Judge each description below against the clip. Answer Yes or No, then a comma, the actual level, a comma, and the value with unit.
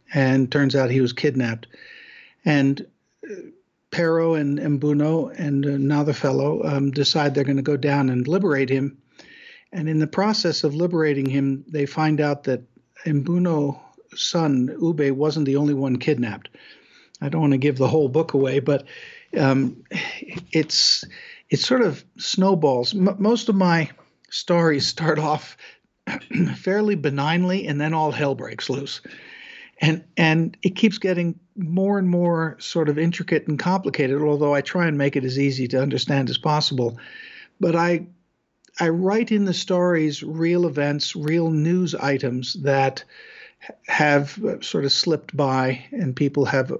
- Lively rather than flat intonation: No, average, 3.9 semitones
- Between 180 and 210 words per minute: No, average, 155 wpm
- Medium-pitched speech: Yes, medium, 150 Hz